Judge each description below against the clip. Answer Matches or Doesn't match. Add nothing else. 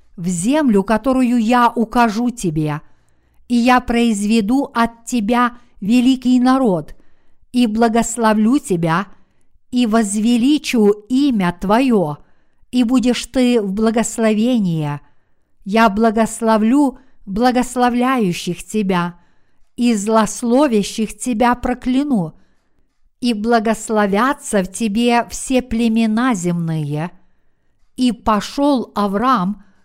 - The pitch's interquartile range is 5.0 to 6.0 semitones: Doesn't match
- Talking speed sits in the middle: Doesn't match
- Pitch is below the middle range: Doesn't match